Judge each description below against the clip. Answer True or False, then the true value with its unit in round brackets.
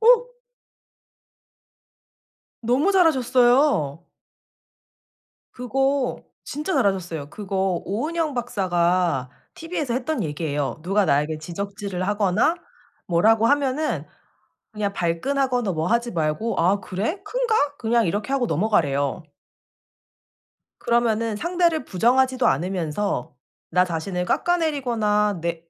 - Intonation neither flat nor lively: False (7.2 semitones)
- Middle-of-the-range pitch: False (210 Hz)